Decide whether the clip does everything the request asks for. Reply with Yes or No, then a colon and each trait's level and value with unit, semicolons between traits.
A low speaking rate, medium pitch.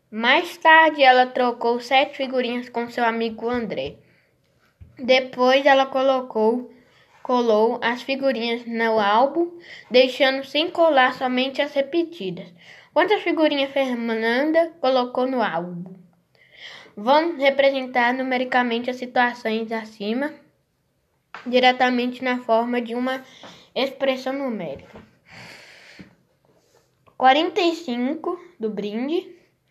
No: slow, 95 wpm; very high, 255 Hz